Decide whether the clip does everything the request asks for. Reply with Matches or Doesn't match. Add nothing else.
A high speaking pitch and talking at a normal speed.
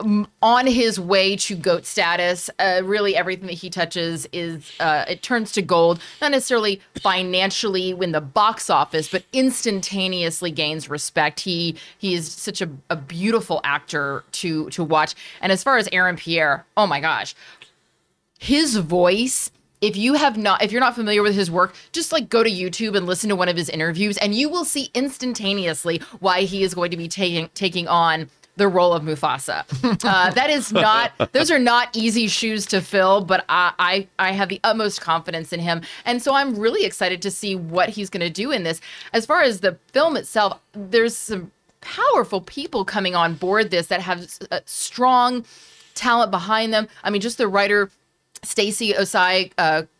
Matches